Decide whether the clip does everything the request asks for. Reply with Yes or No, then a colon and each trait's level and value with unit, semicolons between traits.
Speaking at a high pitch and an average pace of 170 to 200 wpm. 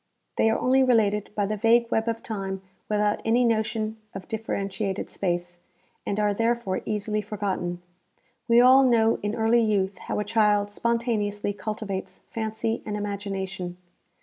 No: high, 210 Hz; average, 150 wpm